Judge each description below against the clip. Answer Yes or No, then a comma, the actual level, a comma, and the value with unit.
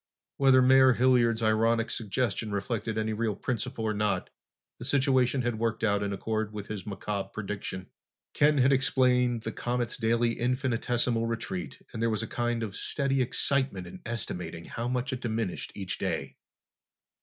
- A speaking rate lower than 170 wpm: Yes, average, 160 wpm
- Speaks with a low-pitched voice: Yes, low, 115 Hz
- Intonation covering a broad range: No, average, 2.9 semitones